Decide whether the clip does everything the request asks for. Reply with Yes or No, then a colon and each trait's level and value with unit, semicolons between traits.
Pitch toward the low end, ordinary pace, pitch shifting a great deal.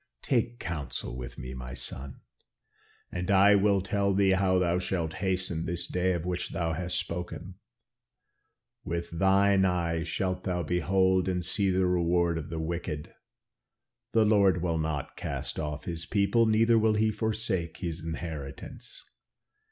No: very low, 90 Hz; average, 150 wpm; average, 2.9 semitones